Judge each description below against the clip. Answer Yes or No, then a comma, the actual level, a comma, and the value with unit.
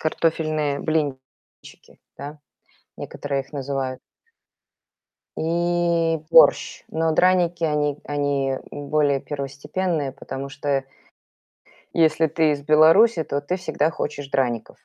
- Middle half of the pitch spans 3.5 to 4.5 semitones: No, narrow, 2.6 semitones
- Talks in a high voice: No, medium, 150 Hz